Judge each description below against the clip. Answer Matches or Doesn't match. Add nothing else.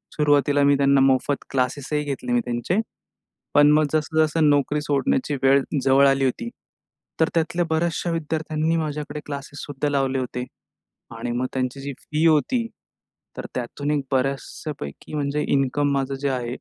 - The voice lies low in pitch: Doesn't match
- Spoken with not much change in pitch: Matches